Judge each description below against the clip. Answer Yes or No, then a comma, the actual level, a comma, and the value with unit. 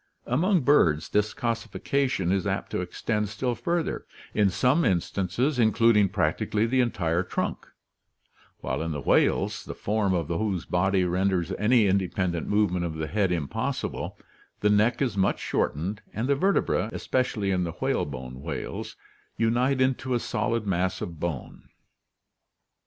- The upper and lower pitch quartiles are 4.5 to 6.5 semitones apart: Yes, average, 5.0 semitones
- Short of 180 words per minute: Yes, average, 150 wpm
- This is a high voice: No, low, 100 Hz